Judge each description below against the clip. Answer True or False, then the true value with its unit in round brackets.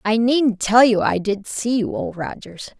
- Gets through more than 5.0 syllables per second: False (4.2 syllables/s)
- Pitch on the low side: False (225 Hz)